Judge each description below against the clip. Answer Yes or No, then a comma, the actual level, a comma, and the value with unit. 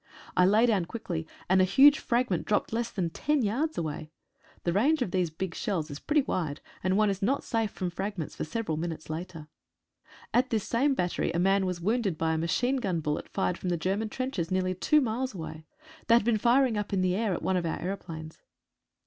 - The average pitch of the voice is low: No, high, 190 Hz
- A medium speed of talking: No, fast, 220 wpm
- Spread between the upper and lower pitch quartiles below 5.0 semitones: No, average, 5.3 semitones